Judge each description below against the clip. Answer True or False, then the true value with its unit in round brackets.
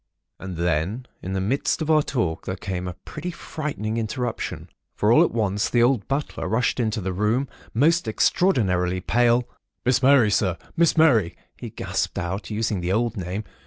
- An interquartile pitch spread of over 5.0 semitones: True (5.4 semitones)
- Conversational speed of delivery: True (180 wpm)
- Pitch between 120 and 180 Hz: False (110 Hz)